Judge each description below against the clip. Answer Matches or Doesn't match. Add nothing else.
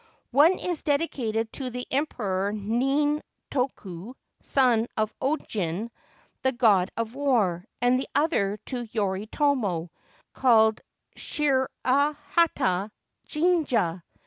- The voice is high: Matches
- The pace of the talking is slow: Matches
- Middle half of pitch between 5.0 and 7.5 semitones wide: Matches